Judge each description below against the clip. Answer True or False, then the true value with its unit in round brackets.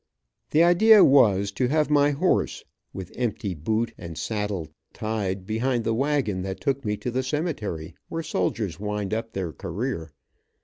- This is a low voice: True (110 Hz)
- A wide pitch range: True (6.0 semitones)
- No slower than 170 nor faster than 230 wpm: False (160 wpm)